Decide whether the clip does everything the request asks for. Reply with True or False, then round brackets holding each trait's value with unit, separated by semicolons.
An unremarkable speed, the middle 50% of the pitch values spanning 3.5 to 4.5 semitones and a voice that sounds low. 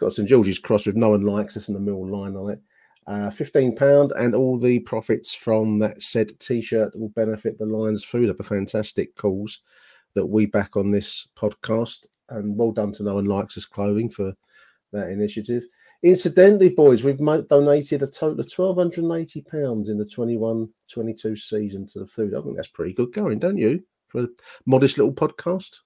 True (195 wpm; 3.9 semitones; 110 Hz)